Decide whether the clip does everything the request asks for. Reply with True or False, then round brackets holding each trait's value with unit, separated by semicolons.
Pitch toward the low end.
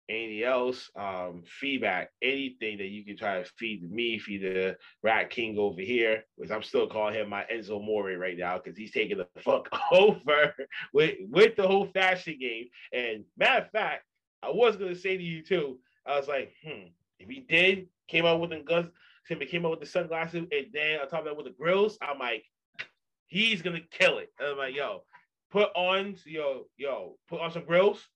False (160 Hz)